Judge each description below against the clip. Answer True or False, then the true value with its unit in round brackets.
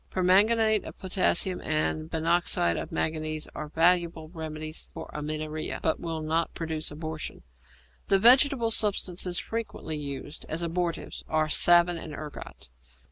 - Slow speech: True (130 wpm)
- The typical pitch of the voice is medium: True (165 Hz)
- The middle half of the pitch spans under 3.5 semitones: True (2.7 semitones)